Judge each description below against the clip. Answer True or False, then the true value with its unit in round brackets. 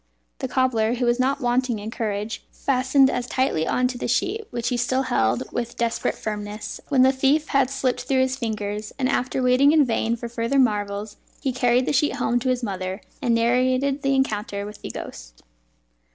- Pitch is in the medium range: False (245 Hz)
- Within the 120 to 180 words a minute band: False (195 wpm)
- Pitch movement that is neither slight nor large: True (3.2 semitones)